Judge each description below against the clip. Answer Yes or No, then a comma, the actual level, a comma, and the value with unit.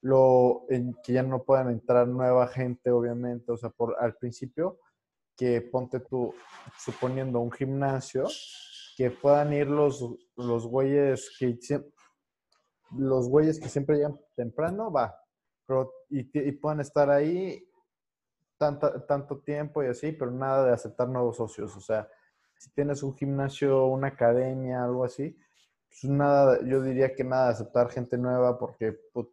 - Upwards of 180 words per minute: No, average, 150 wpm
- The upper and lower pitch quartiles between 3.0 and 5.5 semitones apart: No, narrow, 2.6 semitones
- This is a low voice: Yes, low, 130 Hz